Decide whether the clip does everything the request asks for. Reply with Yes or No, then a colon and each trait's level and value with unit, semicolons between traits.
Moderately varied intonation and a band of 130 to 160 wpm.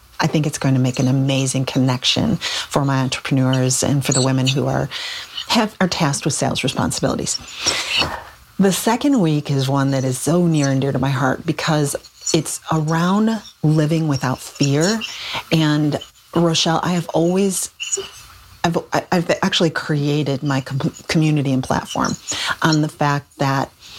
Yes: average, 3.6 semitones; average, 155 wpm